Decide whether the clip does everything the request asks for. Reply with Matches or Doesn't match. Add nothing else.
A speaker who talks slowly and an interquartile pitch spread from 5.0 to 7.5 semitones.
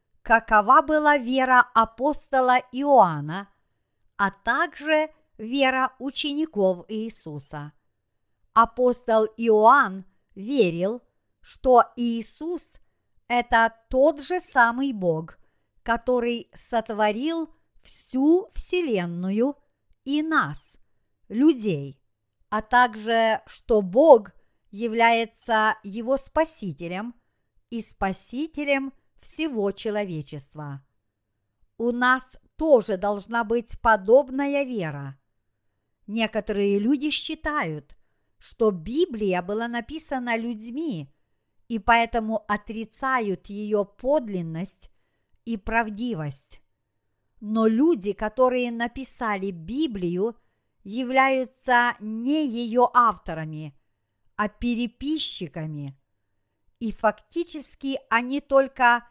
Matches